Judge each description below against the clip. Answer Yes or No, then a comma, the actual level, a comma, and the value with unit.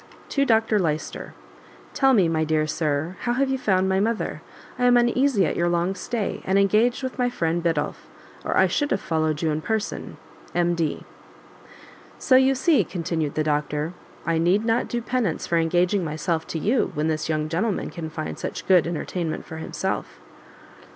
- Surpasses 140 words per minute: Yes, average, 180 wpm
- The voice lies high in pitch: No, medium, 175 Hz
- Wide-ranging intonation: Yes, wide, 6.2 semitones